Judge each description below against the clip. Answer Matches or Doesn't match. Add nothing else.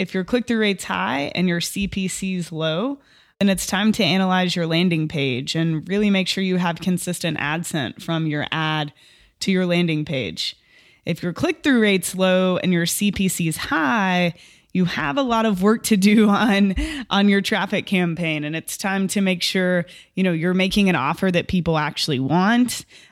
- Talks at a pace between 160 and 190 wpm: Matches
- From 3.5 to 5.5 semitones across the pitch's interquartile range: Doesn't match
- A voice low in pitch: Doesn't match